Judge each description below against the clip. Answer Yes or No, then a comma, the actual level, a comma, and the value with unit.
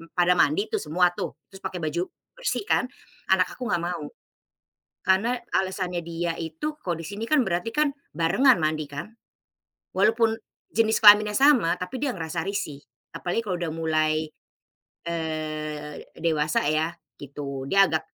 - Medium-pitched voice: Yes, medium, 175 Hz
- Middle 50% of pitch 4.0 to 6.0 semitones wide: Yes, average, 4.7 semitones